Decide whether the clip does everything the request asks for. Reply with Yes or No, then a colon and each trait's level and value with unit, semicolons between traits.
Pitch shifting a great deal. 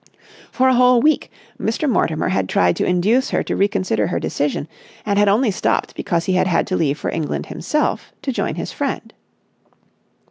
Yes: wide, 7.4 semitones